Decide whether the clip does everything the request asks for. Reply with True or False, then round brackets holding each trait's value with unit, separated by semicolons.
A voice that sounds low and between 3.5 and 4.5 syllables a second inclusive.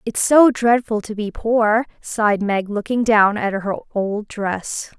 False (215 Hz; 3.8 syllables/s)